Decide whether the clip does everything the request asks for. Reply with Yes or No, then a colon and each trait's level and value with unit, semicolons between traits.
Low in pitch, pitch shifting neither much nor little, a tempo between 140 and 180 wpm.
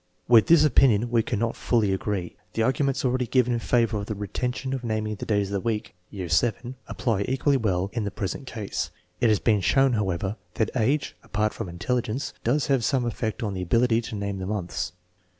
No: low, 115 Hz; average, 3.6 semitones; fast, 205 wpm